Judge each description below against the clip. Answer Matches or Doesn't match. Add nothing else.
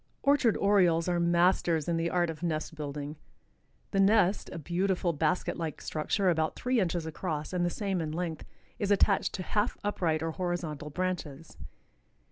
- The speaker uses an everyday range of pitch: Matches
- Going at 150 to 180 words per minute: Matches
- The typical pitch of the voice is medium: Matches